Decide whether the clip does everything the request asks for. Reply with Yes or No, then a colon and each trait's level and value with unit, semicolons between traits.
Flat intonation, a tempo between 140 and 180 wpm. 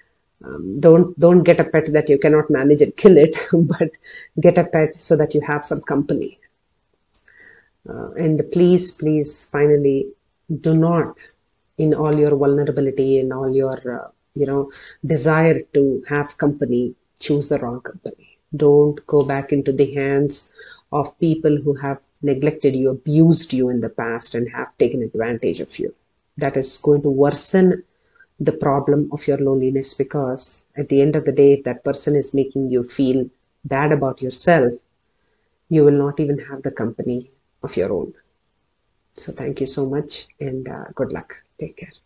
Yes: narrow, 2.1 semitones; average, 170 wpm